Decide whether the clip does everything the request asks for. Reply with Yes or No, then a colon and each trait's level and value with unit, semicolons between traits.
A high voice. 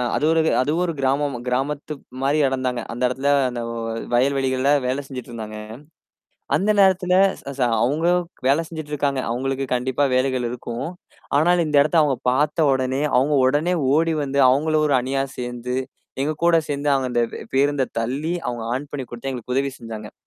No: low, 135 Hz